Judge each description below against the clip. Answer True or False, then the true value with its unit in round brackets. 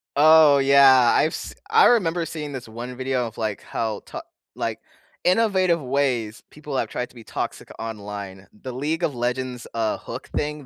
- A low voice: True (130 Hz)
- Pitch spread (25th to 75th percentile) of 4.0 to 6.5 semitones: True (4.7 semitones)